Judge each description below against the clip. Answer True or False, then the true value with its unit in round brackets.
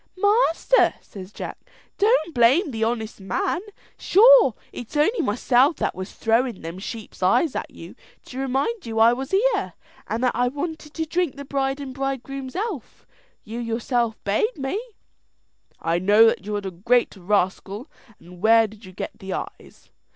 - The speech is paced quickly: False (170 wpm)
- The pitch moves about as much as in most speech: False (6.1 semitones)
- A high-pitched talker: True (245 Hz)